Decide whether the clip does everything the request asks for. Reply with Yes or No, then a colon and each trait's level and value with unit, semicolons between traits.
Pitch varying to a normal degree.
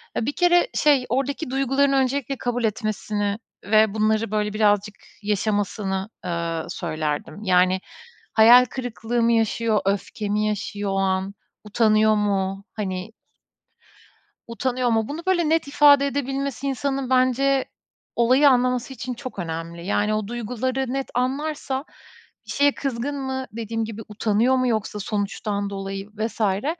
Yes: average, 4.3 semitones